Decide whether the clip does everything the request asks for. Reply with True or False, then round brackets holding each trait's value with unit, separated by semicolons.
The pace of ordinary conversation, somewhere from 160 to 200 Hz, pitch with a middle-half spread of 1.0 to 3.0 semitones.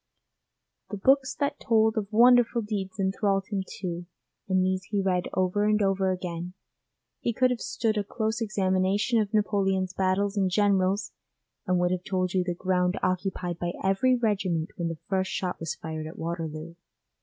True (170 wpm; 190 Hz; 2.5 semitones)